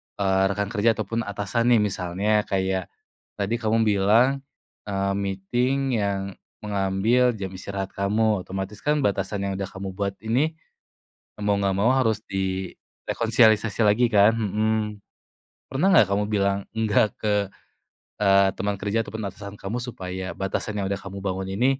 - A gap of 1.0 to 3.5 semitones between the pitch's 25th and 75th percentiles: Yes, narrow, 2.4 semitones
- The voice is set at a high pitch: No, low, 100 Hz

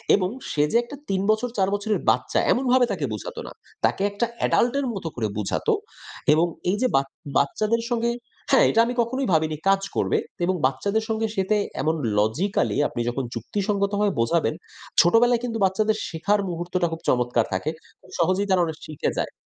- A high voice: Yes, high, 195 Hz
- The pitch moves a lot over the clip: Yes, wide, 5.7 semitones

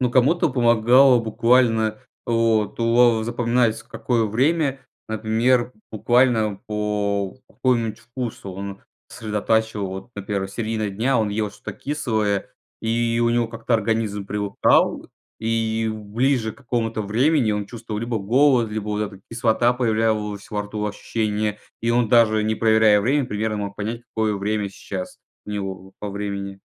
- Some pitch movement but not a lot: No, narrow, 2.3 semitones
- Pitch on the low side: Yes, low, 110 Hz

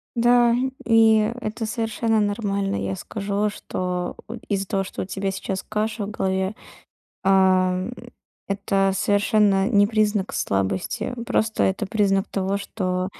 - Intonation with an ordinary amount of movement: No, narrow, 2.2 semitones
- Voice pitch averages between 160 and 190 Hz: No, high, 200 Hz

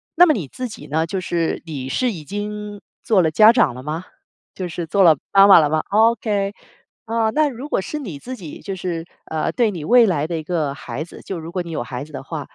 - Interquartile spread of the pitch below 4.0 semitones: No, wide, 5.4 semitones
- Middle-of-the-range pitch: Yes, medium, 180 Hz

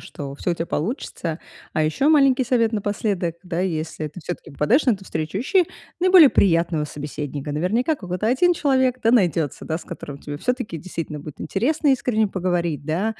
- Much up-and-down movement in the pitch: Yes, wide, 7.9 semitones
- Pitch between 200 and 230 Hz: No, medium, 185 Hz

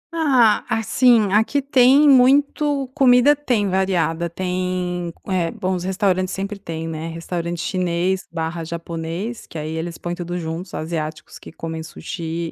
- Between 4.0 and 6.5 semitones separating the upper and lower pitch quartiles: Yes, average, 5.1 semitones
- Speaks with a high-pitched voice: No, medium, 180 Hz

